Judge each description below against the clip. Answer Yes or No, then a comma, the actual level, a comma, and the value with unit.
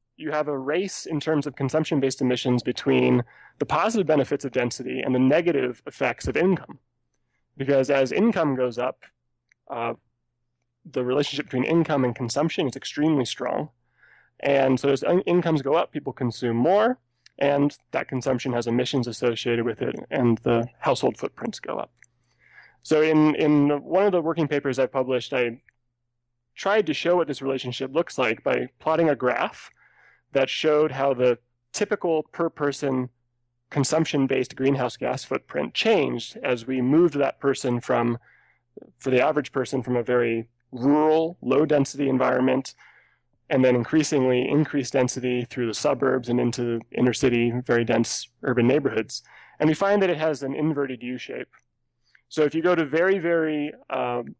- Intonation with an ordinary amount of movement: Yes, average, 3.6 semitones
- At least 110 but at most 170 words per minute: Yes, average, 165 wpm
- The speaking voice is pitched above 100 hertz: Yes, low, 135 Hz